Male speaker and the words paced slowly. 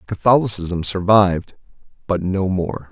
Yes: male; slow, 105 wpm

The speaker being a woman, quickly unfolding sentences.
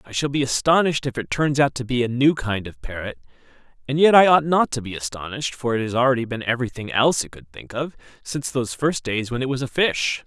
No: male; fast, 250 wpm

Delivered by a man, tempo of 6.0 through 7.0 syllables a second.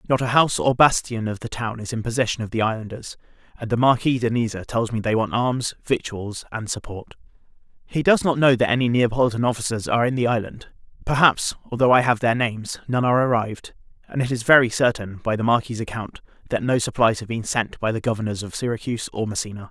Yes: male; 6.2 syllables/s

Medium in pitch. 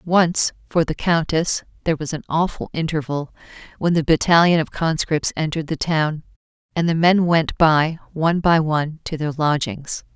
Yes: medium, 160 Hz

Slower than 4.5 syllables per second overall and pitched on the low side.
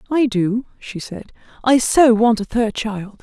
No: 4.0 syllables/s; high, 225 Hz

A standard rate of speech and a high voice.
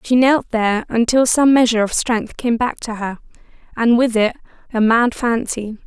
Yes: average, 185 wpm; high, 235 Hz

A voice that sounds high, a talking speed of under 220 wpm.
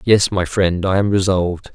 No: very low, 95 Hz; fast, 205 wpm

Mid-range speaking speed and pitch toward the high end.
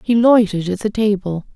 Yes: average, 195 wpm; high, 205 Hz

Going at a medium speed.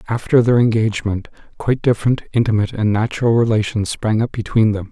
Yes: average, 160 wpm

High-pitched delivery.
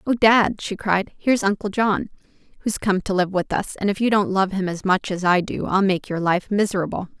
Yes: high, 195 Hz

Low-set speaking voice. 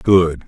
Yes: very low, 85 Hz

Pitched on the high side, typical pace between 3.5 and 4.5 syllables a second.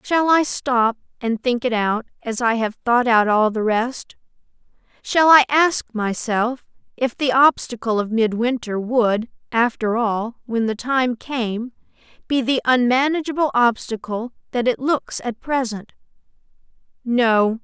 Yes: high, 240 Hz; 3.9 syllables/s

